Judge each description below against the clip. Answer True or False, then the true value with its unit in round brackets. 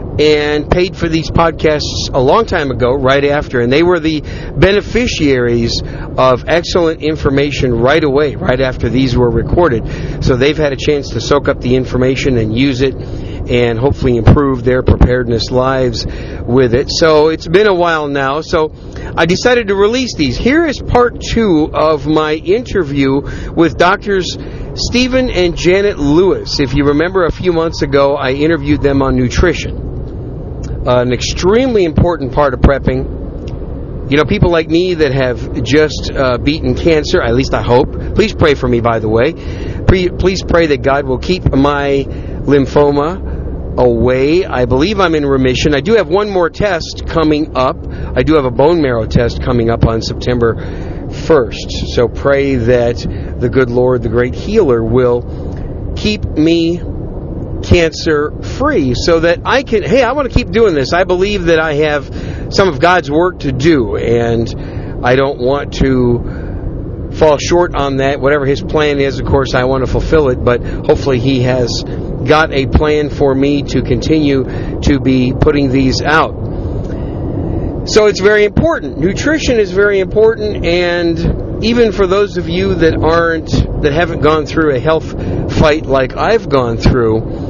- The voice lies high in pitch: False (140 Hz)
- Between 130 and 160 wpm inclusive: False (170 wpm)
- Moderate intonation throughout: True (4.8 semitones)